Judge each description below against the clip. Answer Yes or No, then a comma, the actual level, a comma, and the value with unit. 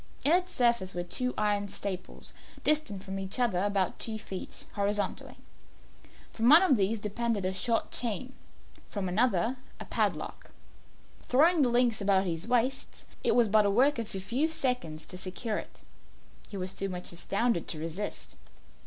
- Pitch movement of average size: Yes, average, 4.5 semitones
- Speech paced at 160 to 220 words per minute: Yes, average, 170 wpm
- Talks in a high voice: Yes, high, 210 Hz